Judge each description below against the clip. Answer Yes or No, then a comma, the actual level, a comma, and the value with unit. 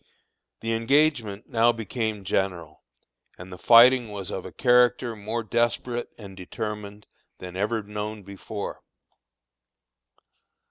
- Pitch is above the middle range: No, low, 110 Hz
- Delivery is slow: Yes, slow, 110 wpm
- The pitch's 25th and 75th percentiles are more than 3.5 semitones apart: No, average, 2.9 semitones